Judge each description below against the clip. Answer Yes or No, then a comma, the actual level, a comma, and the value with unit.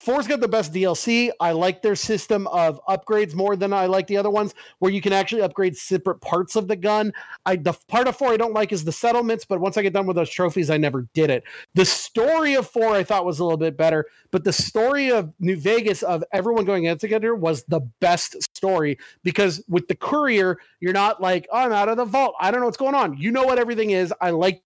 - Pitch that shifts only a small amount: No, average, 3.8 semitones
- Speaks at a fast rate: Yes, fast, 250 wpm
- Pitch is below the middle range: No, high, 195 Hz